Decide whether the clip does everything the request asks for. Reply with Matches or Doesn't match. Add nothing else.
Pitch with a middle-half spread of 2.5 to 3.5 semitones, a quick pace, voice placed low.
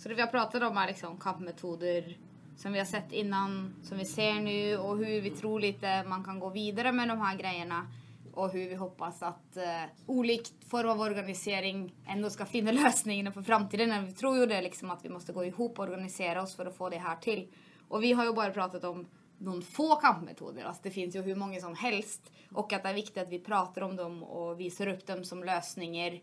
Doesn't match